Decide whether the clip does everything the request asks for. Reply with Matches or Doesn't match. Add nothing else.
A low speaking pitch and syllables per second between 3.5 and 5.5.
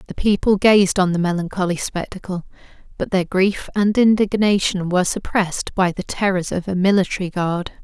Doesn't match